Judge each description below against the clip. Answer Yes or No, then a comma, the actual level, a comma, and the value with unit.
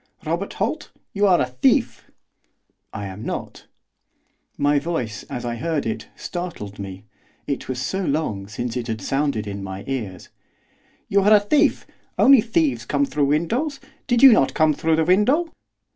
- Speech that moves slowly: No, average, 170 wpm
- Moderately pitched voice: Yes, medium, 145 Hz